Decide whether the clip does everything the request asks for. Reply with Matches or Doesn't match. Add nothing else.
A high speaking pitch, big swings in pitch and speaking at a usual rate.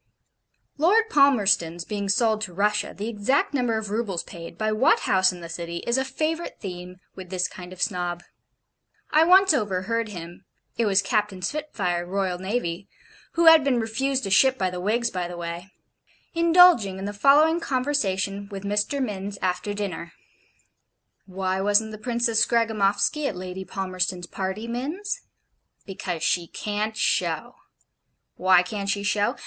Doesn't match